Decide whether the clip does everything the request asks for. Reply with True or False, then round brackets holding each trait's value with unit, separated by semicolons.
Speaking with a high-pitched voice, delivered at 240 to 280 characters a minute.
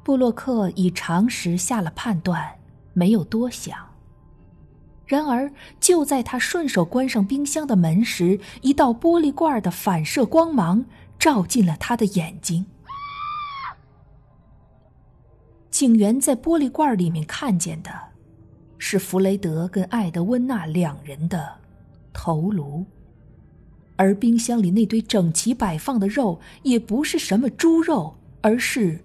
False (220 Hz; 190 characters per minute)